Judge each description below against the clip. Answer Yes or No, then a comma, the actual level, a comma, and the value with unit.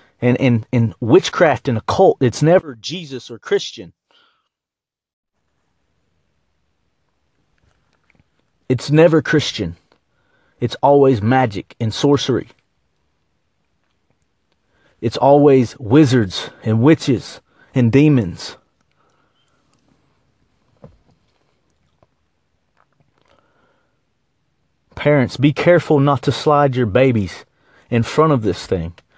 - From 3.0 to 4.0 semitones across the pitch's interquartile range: No, wide, 5.6 semitones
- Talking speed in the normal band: No, slow, 80 wpm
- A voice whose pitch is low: Yes, low, 130 Hz